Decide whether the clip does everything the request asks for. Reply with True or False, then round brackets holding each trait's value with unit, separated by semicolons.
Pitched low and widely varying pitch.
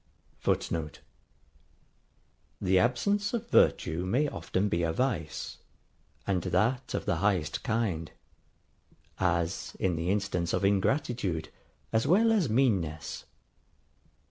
True (95 Hz; 6.8 semitones)